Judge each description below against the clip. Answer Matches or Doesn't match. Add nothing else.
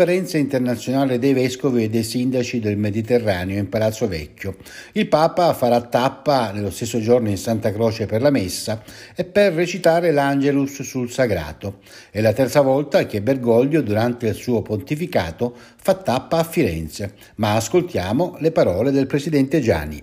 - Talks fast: Doesn't match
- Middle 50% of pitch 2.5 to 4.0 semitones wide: Doesn't match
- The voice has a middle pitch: Doesn't match